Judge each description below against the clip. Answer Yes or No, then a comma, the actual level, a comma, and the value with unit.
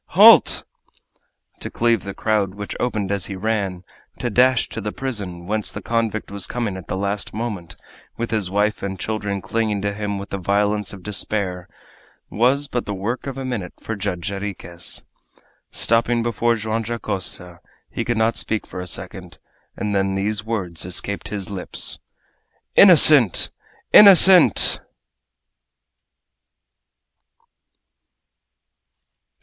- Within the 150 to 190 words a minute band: No, slow, 135 wpm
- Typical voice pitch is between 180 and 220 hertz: No, low, 105 Hz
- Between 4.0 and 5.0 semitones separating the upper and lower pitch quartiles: No, average, 3.0 semitones